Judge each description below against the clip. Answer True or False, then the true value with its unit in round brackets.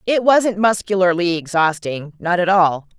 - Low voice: False (180 Hz)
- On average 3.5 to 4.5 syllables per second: True (4.4 syllables/s)